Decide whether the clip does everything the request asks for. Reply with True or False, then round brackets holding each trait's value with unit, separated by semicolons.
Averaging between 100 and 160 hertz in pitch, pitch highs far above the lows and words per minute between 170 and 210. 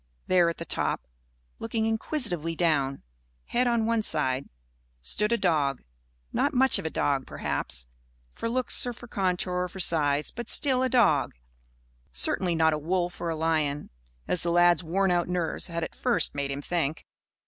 False (175 Hz; 6.2 semitones; 175 wpm)